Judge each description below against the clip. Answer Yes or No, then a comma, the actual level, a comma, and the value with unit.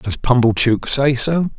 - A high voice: No, low, 125 Hz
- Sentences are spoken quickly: No, average, 150 wpm